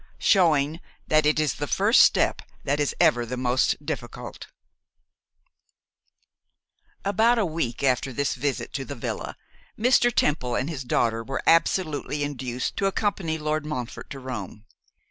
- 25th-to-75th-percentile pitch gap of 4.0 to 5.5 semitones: Yes, average, 4.5 semitones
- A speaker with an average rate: Yes, average, 145 wpm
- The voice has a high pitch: No, medium, 145 Hz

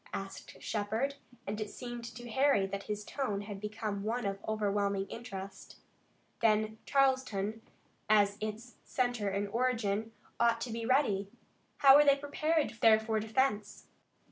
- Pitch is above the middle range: Yes, high, 220 Hz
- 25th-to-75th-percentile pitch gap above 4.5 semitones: No, average, 3.2 semitones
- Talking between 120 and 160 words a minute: Yes, average, 145 wpm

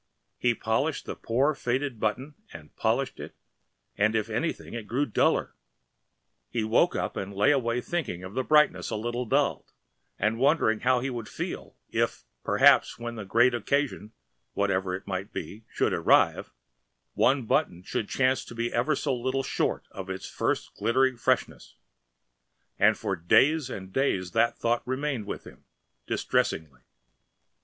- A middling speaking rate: Yes, average, 155 wpm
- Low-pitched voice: Yes, low, 115 Hz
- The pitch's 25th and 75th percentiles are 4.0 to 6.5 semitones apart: Yes, average, 4.4 semitones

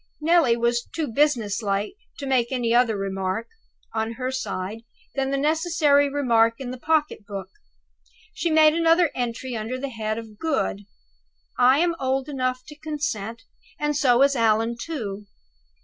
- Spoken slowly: No, average, 155 wpm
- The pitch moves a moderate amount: Yes, average, 4.6 semitones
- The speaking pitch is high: Yes, very high, 255 Hz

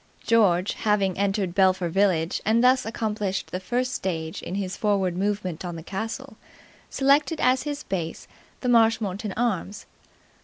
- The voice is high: Yes, high, 200 Hz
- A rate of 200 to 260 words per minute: No, average, 145 wpm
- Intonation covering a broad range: No, average, 3.7 semitones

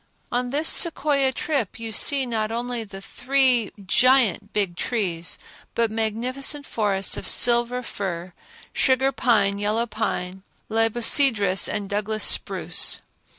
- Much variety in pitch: No, average, 3.8 semitones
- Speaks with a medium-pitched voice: No, high, 225 Hz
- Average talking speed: No, slow, 115 wpm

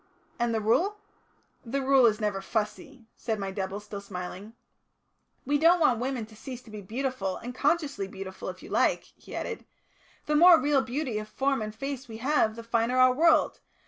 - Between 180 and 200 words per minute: Yes, average, 190 wpm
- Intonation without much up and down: No, average, 4.6 semitones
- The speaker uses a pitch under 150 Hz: No, high, 235 Hz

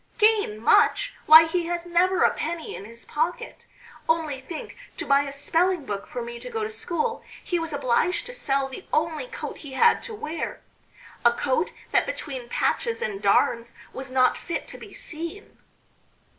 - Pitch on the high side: Yes, very high, 320 Hz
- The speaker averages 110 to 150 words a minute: No, average, 180 wpm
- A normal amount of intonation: No, wide, 5.8 semitones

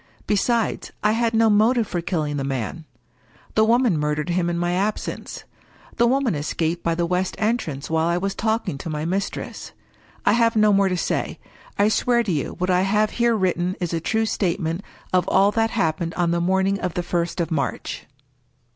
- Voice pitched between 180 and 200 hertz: Yes, medium, 185 Hz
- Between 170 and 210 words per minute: Yes, average, 200 wpm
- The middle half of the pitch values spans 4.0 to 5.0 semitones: Yes, average, 4.4 semitones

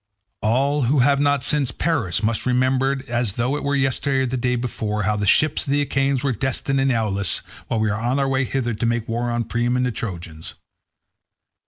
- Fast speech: Yes, fast, 215 wpm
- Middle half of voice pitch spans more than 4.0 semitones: No, average, 3.1 semitones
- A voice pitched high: No, low, 125 Hz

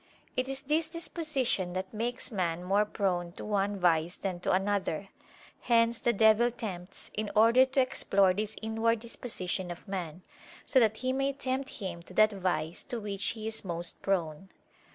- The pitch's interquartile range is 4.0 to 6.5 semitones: Yes, average, 4.4 semitones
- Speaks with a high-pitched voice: Yes, high, 205 Hz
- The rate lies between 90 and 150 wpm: No, average, 175 wpm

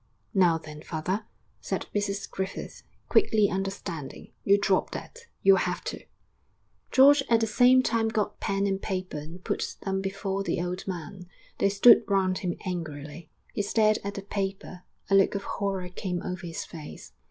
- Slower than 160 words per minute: No, average, 165 wpm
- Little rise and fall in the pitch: Yes, narrow, 2.2 semitones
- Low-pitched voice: No, high, 195 Hz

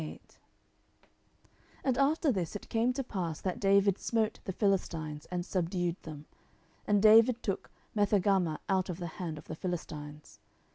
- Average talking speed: Yes, average, 150 wpm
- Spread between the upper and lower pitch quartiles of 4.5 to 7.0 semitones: No, average, 4.1 semitones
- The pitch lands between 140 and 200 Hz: Yes, high, 190 Hz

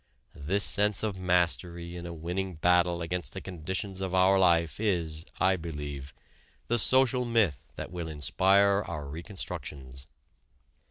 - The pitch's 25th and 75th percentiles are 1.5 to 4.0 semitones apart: Yes, average, 3.0 semitones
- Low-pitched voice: Yes, very low, 90 Hz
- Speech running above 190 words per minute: No, average, 140 wpm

